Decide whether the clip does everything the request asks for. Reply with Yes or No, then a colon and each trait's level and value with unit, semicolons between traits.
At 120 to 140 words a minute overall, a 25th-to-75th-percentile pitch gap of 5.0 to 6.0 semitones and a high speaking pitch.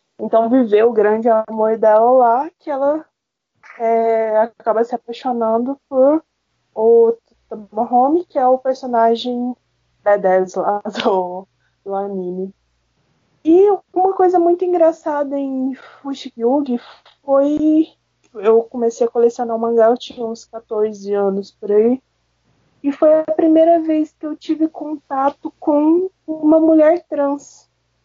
Yes: average, 130 wpm; wide, 5.4 semitones; high, 245 Hz